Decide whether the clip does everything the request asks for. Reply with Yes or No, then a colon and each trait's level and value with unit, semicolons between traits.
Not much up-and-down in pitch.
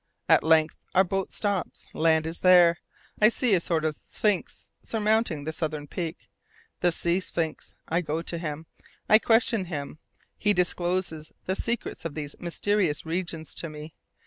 No: average, 3.1 semitones